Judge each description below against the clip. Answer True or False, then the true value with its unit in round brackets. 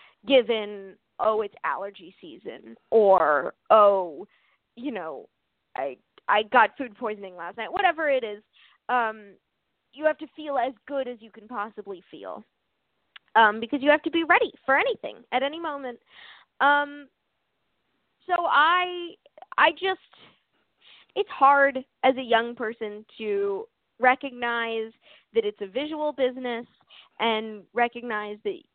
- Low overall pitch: False (250 Hz)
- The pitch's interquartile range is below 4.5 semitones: False (5.5 semitones)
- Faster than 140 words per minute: False (135 wpm)